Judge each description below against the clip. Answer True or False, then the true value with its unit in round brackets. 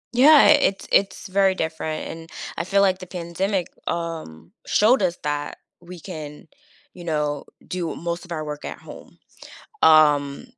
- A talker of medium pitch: True (170 Hz)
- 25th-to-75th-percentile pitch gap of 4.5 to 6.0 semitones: False (3.5 semitones)